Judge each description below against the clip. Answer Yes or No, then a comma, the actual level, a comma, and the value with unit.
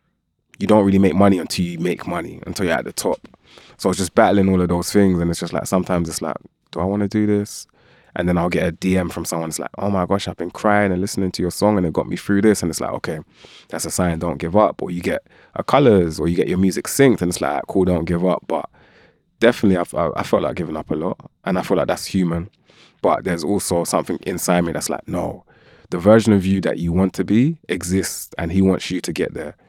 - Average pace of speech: No, fast, 265 wpm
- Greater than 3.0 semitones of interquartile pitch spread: No, narrow, 2.5 semitones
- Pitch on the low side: Yes, very low, 90 Hz